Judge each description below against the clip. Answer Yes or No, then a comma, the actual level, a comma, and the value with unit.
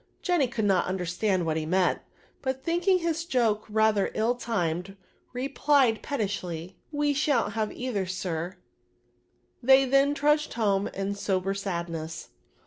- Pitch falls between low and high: No, high, 220 Hz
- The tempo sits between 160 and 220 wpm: No, average, 145 wpm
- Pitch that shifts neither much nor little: No, wide, 6.3 semitones